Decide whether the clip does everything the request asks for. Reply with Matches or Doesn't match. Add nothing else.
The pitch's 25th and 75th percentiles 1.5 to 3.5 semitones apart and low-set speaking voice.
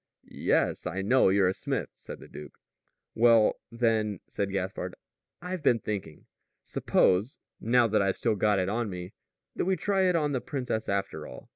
Doesn't match